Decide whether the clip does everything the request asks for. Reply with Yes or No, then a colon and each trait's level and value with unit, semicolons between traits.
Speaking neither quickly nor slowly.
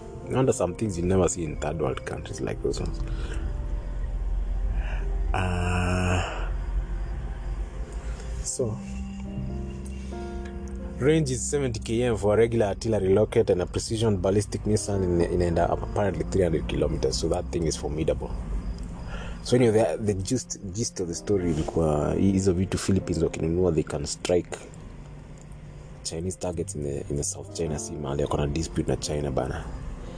Yes: average, 120 wpm